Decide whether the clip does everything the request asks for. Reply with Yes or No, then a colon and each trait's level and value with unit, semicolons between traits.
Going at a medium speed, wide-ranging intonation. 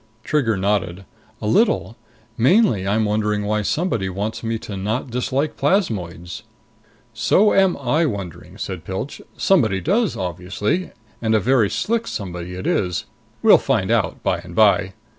Yes: average, 145 wpm; wide, 7.0 semitones